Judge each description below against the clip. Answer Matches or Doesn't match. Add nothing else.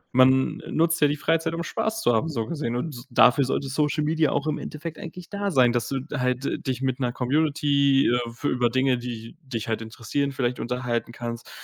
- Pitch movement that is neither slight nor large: Matches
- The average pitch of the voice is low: Matches